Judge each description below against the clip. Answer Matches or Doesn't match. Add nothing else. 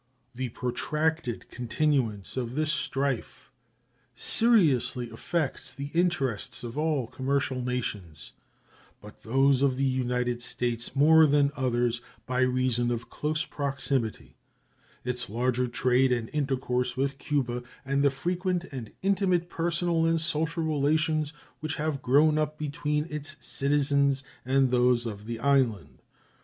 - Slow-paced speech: Matches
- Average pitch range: Matches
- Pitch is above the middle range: Doesn't match